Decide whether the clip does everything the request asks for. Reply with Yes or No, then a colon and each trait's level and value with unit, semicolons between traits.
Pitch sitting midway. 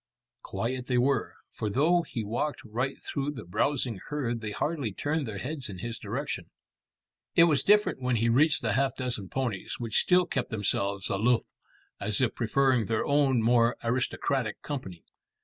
No: low, 125 Hz